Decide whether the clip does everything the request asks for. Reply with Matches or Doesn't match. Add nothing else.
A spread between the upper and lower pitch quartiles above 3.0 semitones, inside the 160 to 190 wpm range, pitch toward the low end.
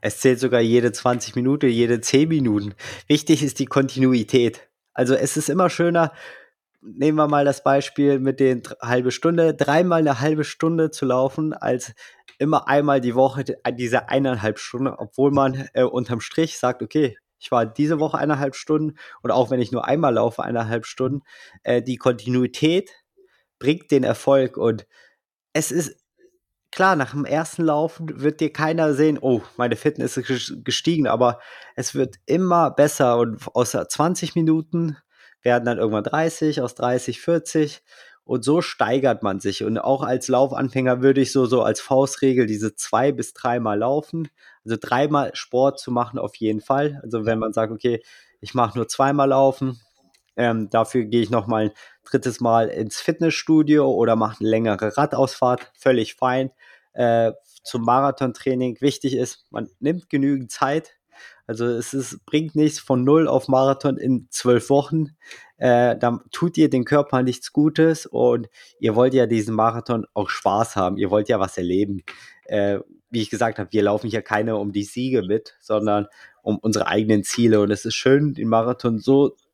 Matches